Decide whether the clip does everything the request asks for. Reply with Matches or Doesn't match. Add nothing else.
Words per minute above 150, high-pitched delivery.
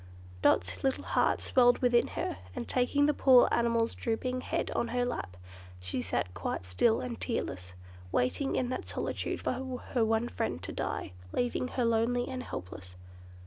Matches